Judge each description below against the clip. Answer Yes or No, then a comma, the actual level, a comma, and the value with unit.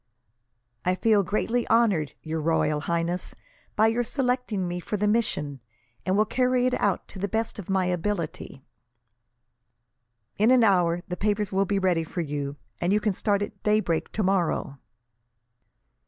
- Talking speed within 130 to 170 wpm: Yes, average, 155 wpm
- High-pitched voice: Yes, high, 195 Hz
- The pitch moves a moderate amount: Yes, average, 4.1 semitones